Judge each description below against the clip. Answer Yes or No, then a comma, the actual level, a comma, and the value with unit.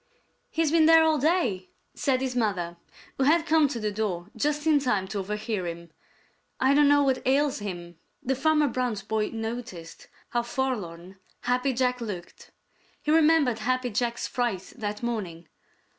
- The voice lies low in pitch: No, high, 240 Hz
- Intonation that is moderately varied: No, wide, 5.8 semitones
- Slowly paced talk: No, average, 160 wpm